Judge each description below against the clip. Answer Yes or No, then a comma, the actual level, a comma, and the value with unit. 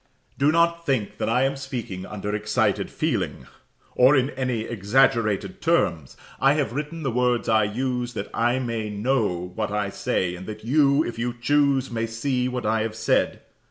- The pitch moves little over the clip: No, average, 4.1 semitones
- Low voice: Yes, low, 120 Hz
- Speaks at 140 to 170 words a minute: No, average, 180 wpm